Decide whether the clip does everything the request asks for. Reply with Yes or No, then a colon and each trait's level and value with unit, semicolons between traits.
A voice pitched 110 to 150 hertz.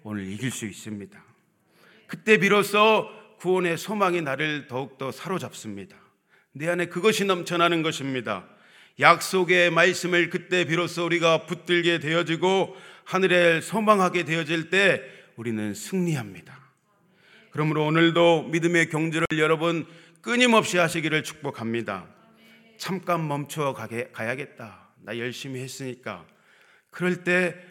No: medium, 170 Hz